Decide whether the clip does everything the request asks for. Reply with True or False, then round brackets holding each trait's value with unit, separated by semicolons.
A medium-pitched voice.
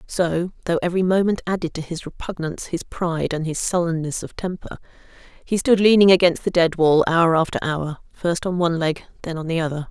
True (170 Hz)